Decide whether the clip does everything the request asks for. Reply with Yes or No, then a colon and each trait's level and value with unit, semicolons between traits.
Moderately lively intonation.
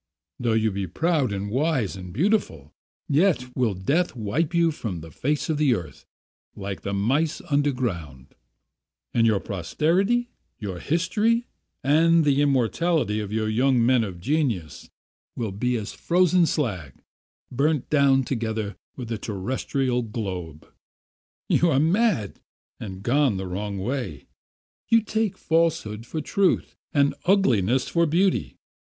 No: wide, 7.7 semitones